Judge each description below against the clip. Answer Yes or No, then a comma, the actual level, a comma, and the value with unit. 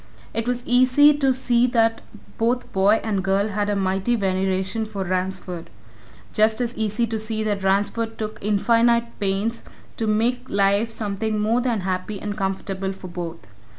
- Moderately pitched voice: No, high, 215 Hz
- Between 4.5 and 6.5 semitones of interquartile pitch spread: No, average, 3.1 semitones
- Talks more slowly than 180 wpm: Yes, average, 160 wpm